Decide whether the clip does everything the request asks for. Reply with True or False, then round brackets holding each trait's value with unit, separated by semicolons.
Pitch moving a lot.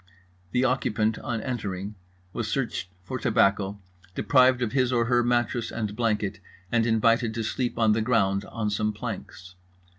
False (2.5 semitones)